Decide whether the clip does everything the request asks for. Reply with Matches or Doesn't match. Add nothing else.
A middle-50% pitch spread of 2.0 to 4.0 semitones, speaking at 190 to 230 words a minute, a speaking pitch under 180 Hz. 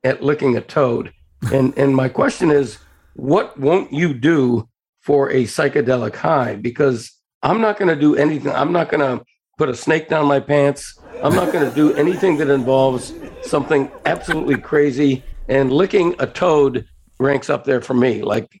Doesn't match